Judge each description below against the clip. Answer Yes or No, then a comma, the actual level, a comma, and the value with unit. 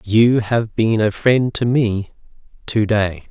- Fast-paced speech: No, average, 165 wpm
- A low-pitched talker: Yes, low, 110 Hz